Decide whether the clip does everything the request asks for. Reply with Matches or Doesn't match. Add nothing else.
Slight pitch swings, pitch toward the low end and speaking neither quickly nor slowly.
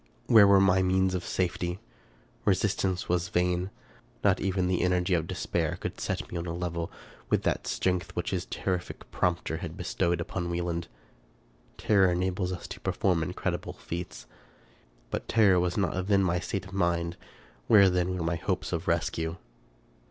Matches